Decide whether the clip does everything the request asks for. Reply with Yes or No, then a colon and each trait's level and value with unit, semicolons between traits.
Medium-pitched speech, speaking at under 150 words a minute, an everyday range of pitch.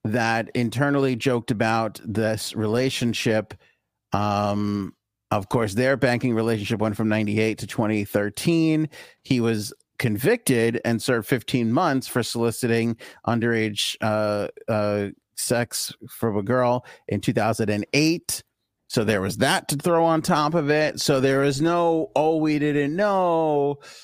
No: low, 115 Hz; average, 140 wpm; average, 4.3 semitones